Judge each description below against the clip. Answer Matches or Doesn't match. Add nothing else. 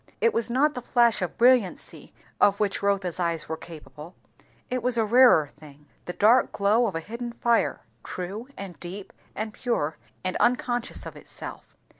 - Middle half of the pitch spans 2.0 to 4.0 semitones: Doesn't match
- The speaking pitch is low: Doesn't match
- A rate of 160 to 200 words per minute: Matches